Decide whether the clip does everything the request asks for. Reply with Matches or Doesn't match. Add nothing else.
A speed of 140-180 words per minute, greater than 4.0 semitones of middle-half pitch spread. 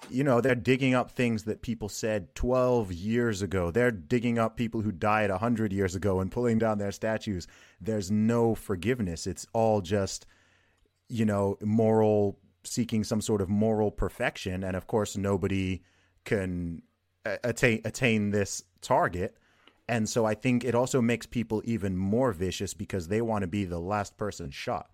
Doesn't match